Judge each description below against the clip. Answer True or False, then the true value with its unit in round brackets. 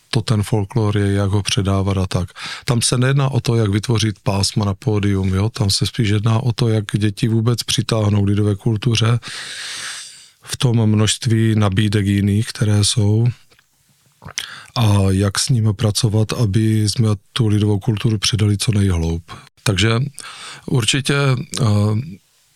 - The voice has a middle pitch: False (110 Hz)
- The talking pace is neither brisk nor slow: True (145 wpm)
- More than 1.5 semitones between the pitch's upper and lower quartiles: True (2.5 semitones)